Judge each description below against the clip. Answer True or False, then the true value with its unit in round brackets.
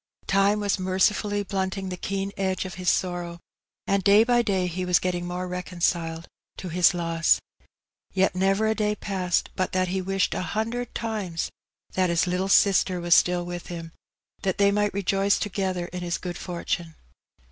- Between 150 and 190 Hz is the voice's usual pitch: True (185 Hz)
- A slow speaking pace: False (175 wpm)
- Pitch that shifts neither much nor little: False (2.0 semitones)